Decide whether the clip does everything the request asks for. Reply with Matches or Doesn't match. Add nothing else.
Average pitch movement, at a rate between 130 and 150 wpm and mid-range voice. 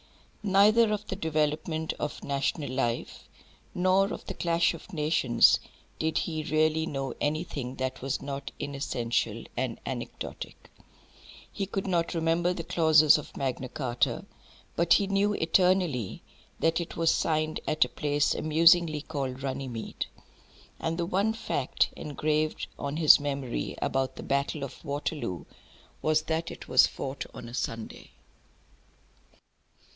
Matches